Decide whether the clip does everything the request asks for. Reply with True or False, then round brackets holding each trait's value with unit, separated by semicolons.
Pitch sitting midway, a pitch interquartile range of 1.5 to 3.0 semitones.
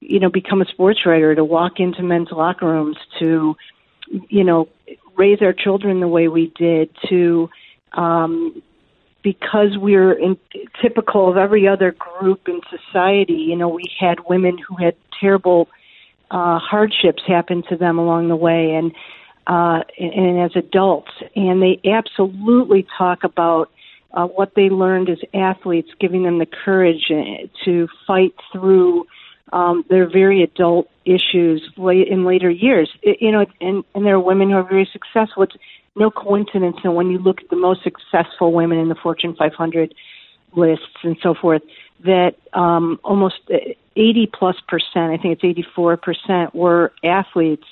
True (180 Hz; 2.4 semitones)